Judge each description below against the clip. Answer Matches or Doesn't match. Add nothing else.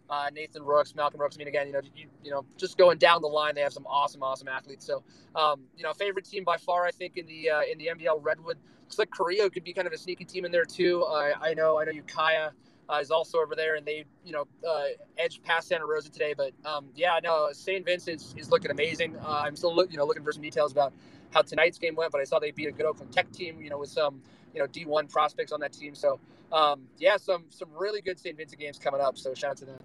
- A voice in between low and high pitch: Matches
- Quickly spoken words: Matches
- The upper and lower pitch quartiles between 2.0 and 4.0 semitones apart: Matches